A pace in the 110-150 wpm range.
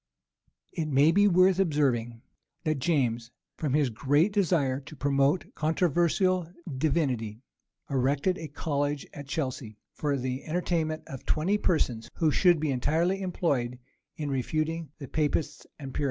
Yes: average, 140 wpm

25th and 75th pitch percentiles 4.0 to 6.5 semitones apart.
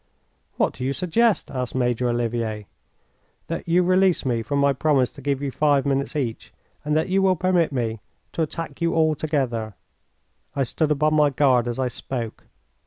Yes: average, 4.3 semitones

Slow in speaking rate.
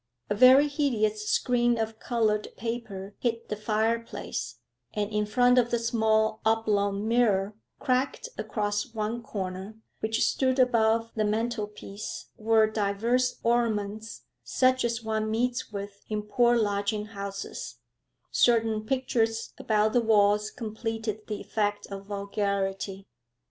Yes: slow, 125 wpm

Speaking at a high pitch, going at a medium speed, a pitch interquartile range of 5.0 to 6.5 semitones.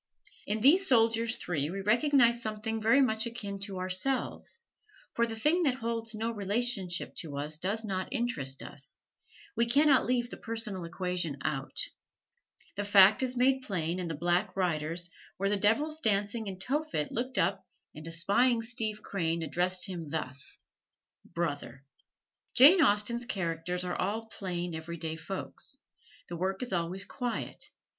Yes: high, 200 Hz; average, 155 wpm; average, 5.3 semitones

